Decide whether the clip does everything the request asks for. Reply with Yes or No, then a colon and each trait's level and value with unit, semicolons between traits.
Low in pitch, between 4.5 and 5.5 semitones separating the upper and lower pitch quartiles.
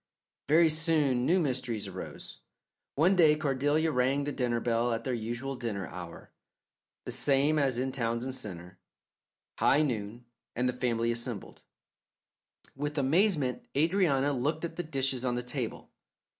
No: low, 130 Hz; average, 4.0 semitones